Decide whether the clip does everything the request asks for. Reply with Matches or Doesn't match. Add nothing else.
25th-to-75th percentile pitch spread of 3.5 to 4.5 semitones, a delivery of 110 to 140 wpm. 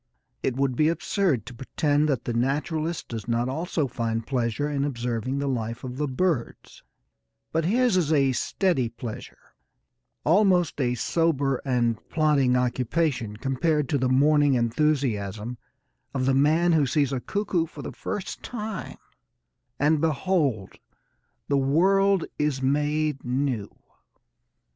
Matches